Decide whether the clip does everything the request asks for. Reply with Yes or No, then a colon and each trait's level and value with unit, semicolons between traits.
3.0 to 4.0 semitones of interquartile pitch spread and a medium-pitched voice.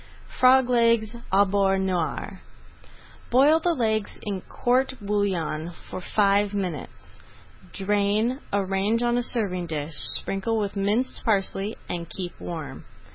No: average, 3.6 semitones; high, 200 Hz